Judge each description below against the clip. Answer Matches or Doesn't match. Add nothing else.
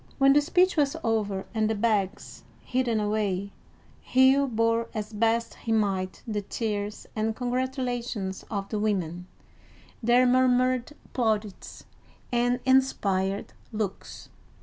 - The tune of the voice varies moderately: Matches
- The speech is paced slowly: Matches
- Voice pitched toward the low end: Doesn't match